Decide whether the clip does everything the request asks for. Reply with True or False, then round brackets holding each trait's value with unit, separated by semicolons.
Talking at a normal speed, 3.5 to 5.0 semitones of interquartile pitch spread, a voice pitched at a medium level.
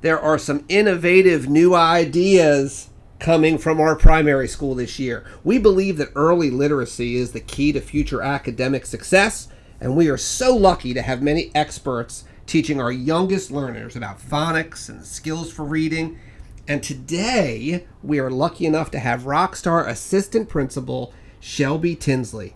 True (155 wpm; 4.6 semitones; 145 Hz)